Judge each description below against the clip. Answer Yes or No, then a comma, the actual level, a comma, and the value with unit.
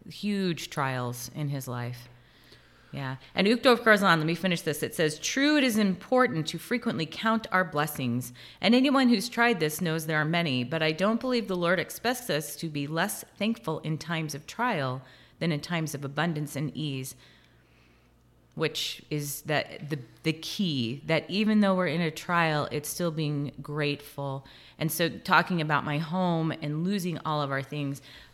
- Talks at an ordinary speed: Yes, average, 180 wpm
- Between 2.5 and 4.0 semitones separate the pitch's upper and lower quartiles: No, average, 4.5 semitones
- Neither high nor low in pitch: Yes, medium, 155 Hz